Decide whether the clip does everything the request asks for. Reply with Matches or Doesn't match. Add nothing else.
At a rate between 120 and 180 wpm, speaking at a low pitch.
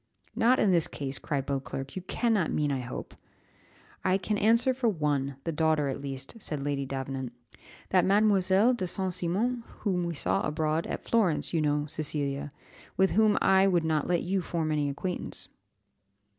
Doesn't match